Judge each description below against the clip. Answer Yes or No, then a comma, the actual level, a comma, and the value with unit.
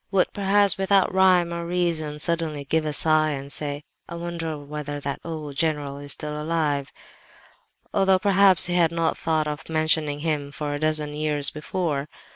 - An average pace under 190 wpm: Yes, average, 170 wpm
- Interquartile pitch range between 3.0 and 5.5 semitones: No, narrow, 2.5 semitones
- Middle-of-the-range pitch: Yes, medium, 155 Hz